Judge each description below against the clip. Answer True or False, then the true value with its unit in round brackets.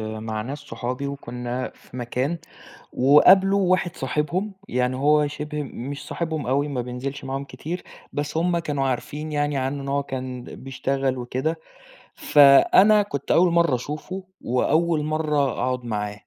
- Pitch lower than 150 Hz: True (140 Hz)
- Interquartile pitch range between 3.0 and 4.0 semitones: True (3.4 semitones)